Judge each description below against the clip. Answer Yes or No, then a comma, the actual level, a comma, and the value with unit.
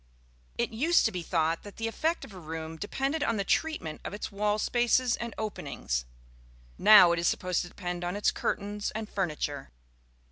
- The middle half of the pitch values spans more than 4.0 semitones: Yes, average, 4.8 semitones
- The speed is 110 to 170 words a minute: No, average, 185 wpm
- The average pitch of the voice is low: No, high, 200 Hz